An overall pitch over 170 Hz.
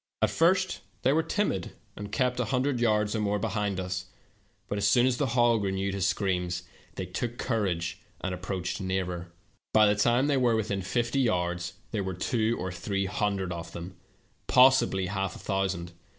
No: low, 100 Hz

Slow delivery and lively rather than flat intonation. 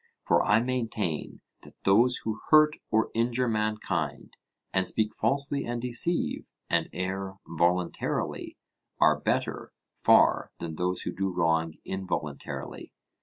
No: slow, 125 wpm; average, 4.8 semitones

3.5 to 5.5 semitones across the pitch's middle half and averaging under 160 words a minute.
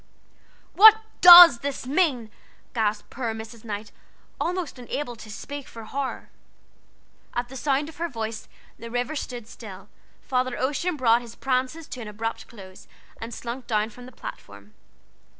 Yes: average, 4.0 semitones; average, 150 wpm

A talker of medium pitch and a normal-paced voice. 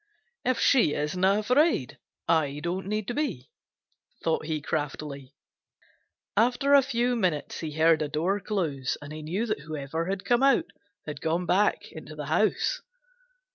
Yes: medium, 170 Hz; average, 150 wpm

